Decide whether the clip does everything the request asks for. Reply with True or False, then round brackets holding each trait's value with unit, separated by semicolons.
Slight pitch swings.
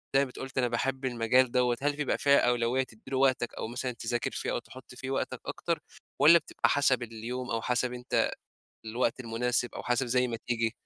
True (1.6 semitones)